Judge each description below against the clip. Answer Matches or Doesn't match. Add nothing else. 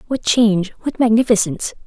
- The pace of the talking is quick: Doesn't match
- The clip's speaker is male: Doesn't match